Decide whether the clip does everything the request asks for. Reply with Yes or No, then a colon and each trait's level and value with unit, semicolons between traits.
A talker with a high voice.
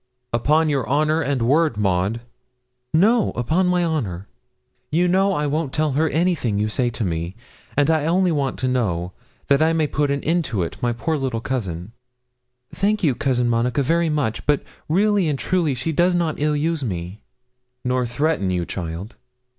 No: medium, 140 Hz